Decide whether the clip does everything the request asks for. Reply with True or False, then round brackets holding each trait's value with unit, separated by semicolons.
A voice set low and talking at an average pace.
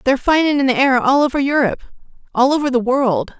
False (265 Hz; 195 wpm)